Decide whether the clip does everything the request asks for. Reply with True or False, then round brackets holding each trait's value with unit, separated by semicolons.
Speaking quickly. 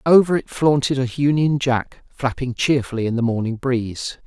False (170 wpm)